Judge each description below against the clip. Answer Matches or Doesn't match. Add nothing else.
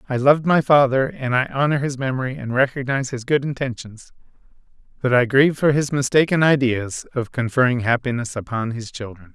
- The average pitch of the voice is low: Matches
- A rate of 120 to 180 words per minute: Matches